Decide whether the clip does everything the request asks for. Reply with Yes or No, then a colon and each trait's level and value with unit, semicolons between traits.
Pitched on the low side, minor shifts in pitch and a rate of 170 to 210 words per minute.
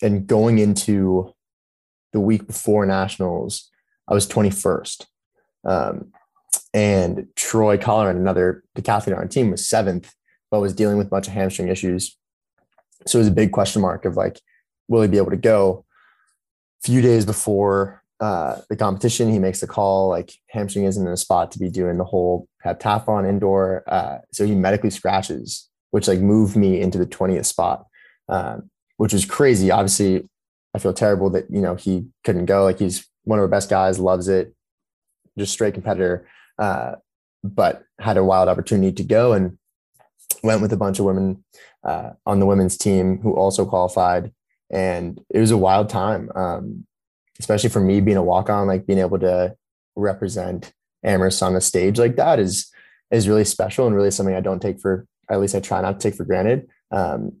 Yes: very low, 95 Hz; narrow, 1.8 semitones; average, 185 wpm